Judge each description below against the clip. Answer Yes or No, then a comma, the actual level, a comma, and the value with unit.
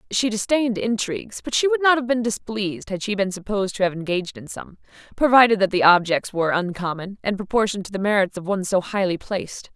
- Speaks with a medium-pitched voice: No, high, 205 Hz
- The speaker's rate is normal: No, fast, 215 wpm